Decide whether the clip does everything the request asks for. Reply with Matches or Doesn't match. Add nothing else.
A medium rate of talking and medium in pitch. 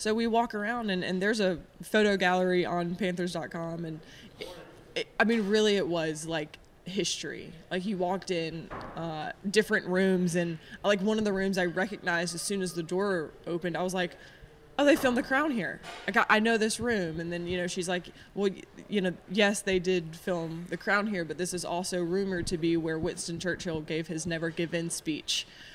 Doesn't match